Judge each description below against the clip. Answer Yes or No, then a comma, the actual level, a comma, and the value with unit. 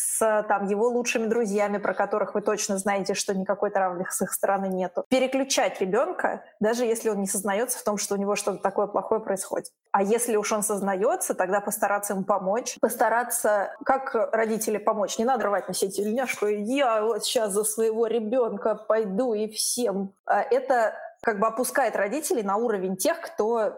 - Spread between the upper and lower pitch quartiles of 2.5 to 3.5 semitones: Yes, average, 2.9 semitones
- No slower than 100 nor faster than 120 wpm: No, fast, 175 wpm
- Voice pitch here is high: Yes, high, 215 Hz